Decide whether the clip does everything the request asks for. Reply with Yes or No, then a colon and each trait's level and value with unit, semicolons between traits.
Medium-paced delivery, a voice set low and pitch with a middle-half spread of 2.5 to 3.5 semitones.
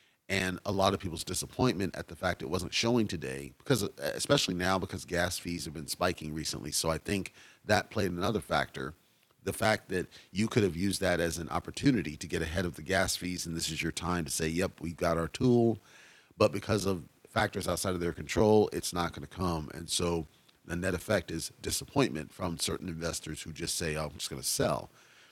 No: fast, 220 wpm; very low, 90 Hz; average, 2.8 semitones